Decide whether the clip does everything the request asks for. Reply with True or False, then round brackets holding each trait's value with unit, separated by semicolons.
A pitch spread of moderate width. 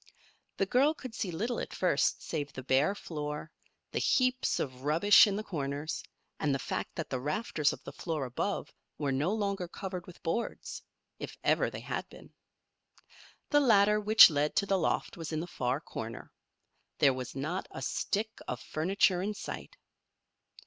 False (6.1 semitones)